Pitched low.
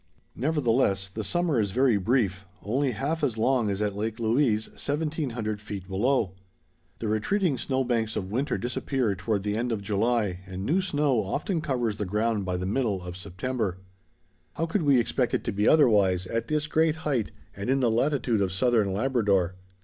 Yes: low, 115 Hz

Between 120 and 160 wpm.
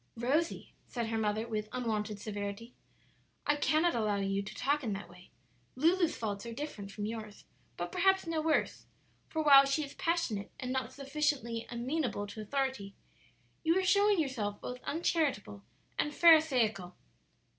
Yes: average, 155 wpm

